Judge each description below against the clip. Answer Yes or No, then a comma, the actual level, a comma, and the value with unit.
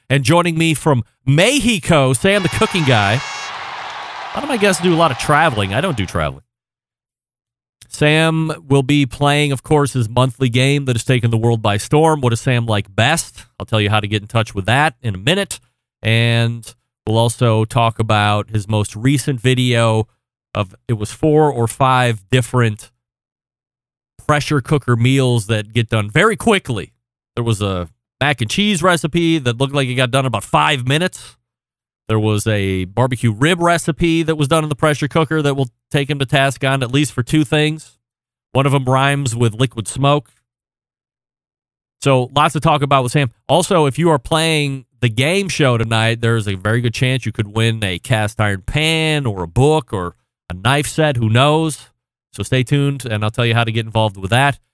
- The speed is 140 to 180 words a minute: No, average, 195 wpm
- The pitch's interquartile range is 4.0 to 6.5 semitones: Yes, average, 4.4 semitones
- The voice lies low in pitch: Yes, low, 125 Hz